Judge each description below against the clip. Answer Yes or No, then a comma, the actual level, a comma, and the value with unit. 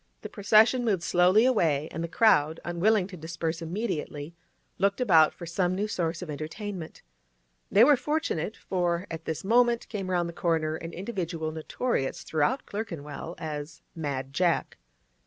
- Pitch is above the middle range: No, medium, 175 Hz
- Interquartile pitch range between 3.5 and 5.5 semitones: Yes, average, 4.6 semitones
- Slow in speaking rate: No, average, 155 wpm